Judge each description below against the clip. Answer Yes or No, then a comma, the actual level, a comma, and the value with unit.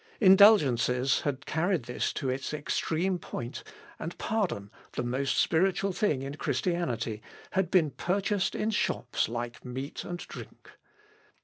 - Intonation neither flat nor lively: No, wide, 6.9 semitones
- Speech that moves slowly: Yes, slow, 130 wpm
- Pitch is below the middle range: No, medium, 155 Hz